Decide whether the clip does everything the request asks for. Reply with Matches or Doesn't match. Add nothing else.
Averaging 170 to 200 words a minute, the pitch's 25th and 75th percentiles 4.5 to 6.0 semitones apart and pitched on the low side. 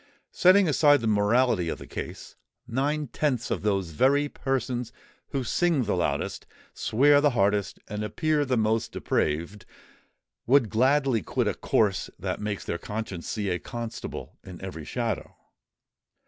Doesn't match